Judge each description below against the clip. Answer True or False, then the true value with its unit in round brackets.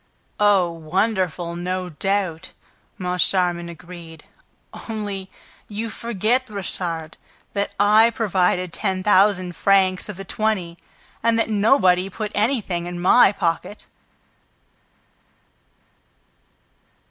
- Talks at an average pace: False (95 wpm)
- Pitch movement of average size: True (3.0 semitones)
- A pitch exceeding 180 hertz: True (190 Hz)